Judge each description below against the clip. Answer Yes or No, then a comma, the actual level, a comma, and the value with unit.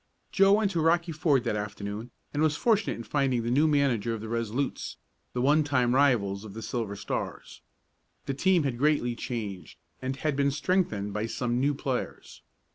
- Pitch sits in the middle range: No, low, 130 Hz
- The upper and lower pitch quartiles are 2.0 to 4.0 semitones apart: No, average, 4.9 semitones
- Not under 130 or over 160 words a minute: No, average, 185 wpm